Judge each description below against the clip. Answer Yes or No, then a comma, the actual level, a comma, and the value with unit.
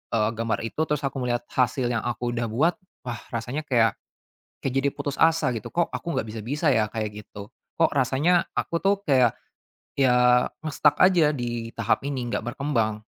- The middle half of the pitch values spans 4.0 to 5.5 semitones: Yes, average, 4.3 semitones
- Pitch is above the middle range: No, low, 125 Hz